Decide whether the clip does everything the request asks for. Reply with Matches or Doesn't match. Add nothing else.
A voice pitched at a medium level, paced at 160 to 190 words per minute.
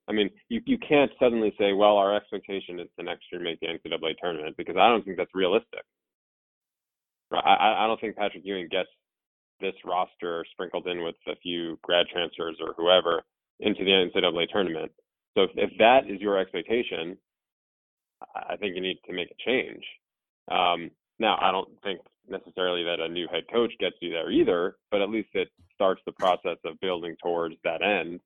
Doesn't match